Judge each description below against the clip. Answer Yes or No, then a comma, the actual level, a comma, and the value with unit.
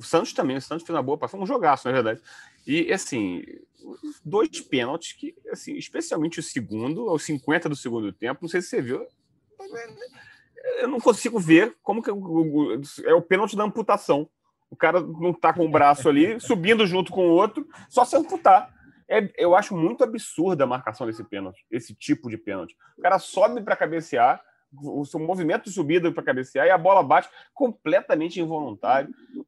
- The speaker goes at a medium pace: No, fast, 190 wpm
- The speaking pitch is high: Yes, high, 200 Hz